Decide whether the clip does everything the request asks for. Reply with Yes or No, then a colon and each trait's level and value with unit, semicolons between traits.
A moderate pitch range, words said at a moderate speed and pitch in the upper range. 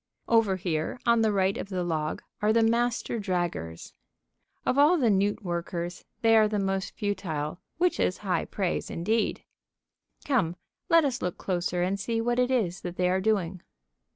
Yes: average, 4.4 semitones; average, 175 wpm; high, 195 Hz